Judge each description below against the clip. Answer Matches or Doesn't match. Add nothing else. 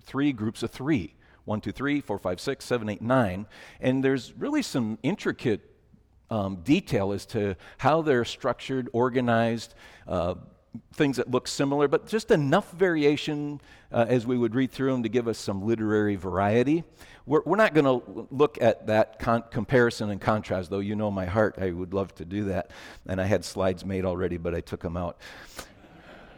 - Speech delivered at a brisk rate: Doesn't match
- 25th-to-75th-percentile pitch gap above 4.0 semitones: Matches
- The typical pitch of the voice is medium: Doesn't match